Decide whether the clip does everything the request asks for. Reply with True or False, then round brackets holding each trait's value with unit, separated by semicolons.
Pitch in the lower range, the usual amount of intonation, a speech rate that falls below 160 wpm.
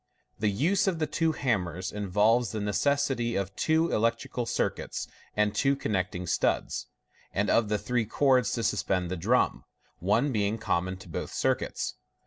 True (110 Hz; 4.9 semitones; 150 wpm)